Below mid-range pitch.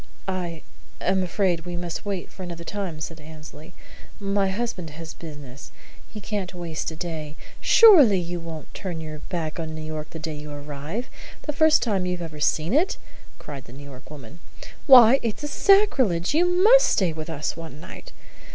No: medium, 170 Hz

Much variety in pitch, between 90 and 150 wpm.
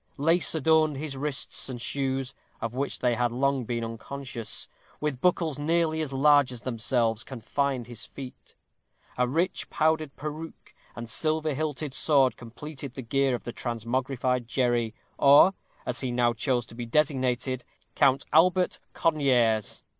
No: average, 3.7 semitones; average, 145 wpm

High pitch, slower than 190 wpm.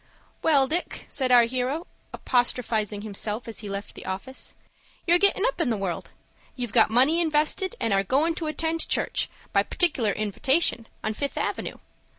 Yes: very high, 255 Hz; average, 165 wpm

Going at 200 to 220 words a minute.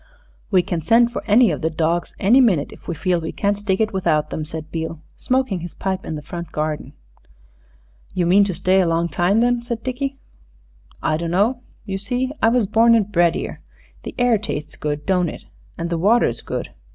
Yes: fast, 205 wpm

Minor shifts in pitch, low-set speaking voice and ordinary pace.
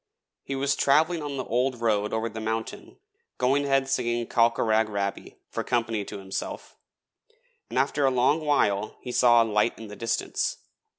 No: average, 3.5 semitones; low, 120 Hz; average, 170 wpm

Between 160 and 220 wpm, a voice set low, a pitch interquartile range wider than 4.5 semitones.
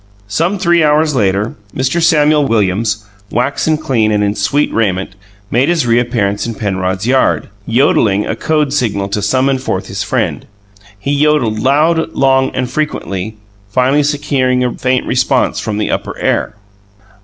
No: average, 150 wpm; low, 125 Hz; wide, 5.4 semitones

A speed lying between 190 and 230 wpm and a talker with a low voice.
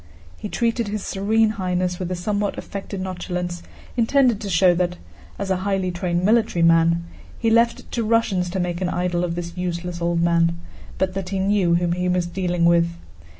No: average, 195 wpm; medium, 180 Hz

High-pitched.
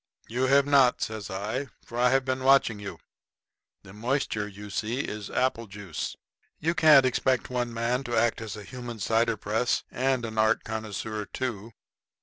No: low, 115 Hz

